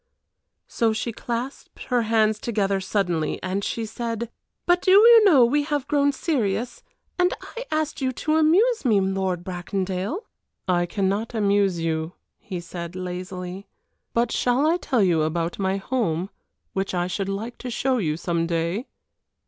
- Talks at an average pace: Yes, average, 155 wpm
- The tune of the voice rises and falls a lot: Yes, wide, 5.9 semitones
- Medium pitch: No, high, 205 Hz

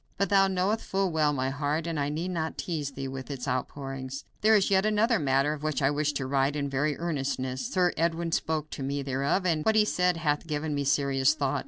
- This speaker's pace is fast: Yes, fast, 230 wpm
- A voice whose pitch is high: No, medium, 150 Hz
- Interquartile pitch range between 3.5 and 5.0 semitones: Yes, average, 3.9 semitones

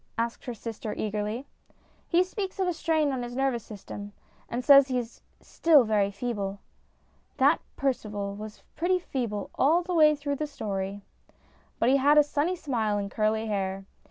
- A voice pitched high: Yes, high, 240 Hz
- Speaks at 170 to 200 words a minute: Yes, average, 175 wpm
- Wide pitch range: Yes, wide, 5.9 semitones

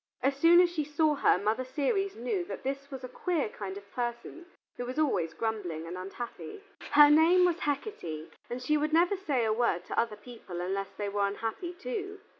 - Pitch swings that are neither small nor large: No, wide, 7.8 semitones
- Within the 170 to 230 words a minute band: Yes, fast, 205 wpm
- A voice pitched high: Yes, very high, 260 Hz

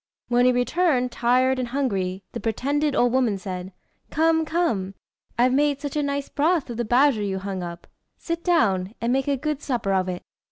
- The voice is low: No, very high, 250 Hz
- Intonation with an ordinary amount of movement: No, wide, 6.2 semitones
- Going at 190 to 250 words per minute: Yes, average, 195 wpm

